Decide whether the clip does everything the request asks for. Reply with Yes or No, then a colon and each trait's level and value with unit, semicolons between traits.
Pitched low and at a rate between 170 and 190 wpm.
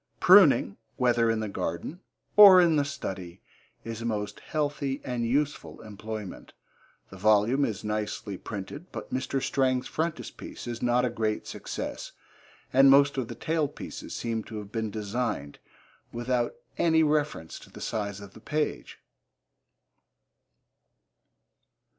No: low, 120 Hz; slow, 135 wpm